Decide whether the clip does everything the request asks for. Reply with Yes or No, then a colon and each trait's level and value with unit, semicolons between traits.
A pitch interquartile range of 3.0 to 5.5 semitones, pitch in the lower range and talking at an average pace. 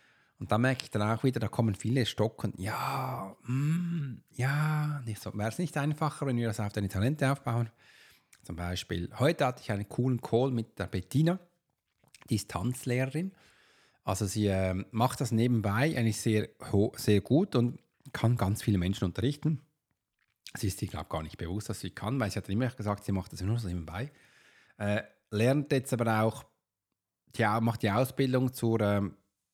Yes: average, 4.4 semitones; low, 115 Hz; average, 175 wpm